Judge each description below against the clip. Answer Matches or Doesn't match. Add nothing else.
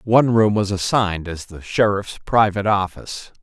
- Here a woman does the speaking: Doesn't match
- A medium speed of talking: Matches